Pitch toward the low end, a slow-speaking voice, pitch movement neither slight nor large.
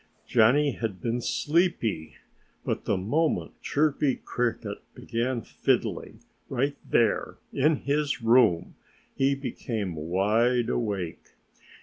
Yes: low, 120 Hz; slow, 100 wpm; average, 4.6 semitones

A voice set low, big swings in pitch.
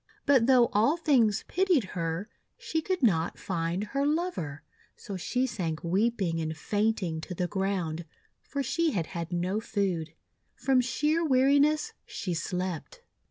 No: high, 210 Hz; wide, 8.3 semitones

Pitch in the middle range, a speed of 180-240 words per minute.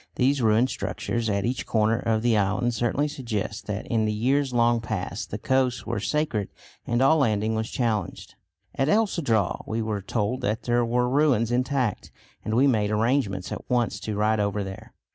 No: low, 115 Hz; average, 185 wpm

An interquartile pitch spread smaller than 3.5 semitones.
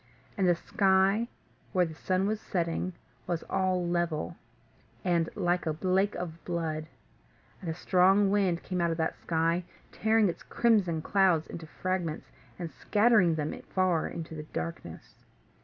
Yes: narrow, 2.6 semitones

